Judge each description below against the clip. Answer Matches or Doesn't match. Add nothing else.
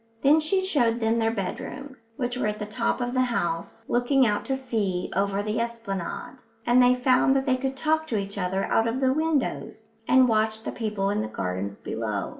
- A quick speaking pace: Matches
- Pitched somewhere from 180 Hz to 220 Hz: Doesn't match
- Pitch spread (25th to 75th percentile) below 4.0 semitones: Doesn't match